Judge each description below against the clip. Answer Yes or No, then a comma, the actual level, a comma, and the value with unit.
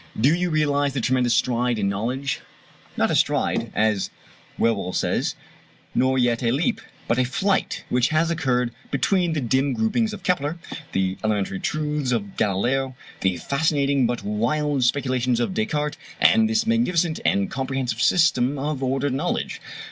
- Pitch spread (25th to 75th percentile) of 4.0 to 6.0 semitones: Yes, average, 4.4 semitones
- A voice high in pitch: No, low, 135 Hz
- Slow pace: No, average, 155 wpm